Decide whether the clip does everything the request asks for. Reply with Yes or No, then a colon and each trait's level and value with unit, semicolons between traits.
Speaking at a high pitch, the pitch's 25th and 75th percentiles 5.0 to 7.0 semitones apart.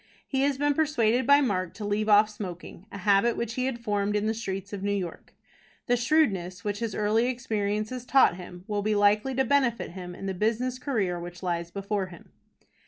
No: high, 210 Hz; average, 4.0 semitones